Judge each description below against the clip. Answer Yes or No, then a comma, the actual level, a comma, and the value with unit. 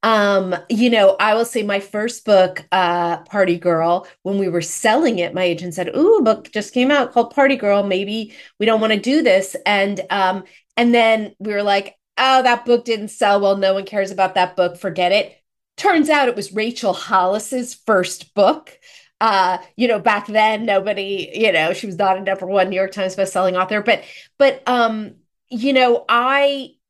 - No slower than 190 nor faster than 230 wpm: Yes, average, 200 wpm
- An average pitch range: Yes, average, 3.9 semitones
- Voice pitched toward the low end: No, high, 205 Hz